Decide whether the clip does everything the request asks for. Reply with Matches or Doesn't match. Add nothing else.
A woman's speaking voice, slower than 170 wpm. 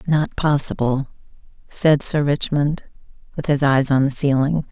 Matches